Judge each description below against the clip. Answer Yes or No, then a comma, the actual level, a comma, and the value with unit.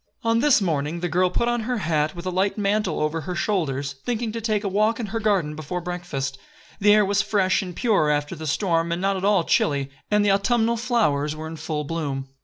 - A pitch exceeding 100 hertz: Yes, medium, 185 Hz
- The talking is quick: Yes, fast, 230 wpm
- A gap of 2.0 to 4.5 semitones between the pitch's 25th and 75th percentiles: No, wide, 5.4 semitones